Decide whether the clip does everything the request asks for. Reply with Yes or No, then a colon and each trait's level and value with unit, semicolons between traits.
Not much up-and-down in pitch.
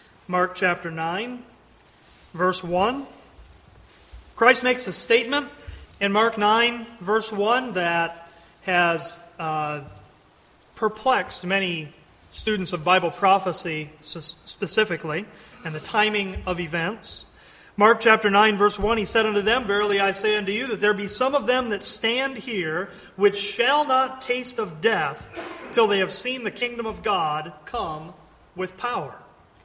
No: average, 4.6 semitones